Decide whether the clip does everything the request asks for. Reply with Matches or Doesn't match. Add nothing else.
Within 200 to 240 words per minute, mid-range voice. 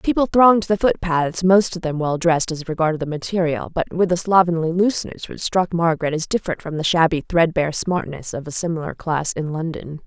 Matches